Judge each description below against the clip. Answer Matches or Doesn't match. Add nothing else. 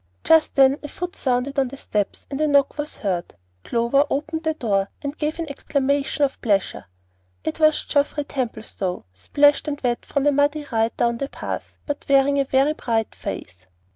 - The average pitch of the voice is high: Matches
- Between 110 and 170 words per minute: Doesn't match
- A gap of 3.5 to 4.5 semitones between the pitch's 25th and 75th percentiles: Matches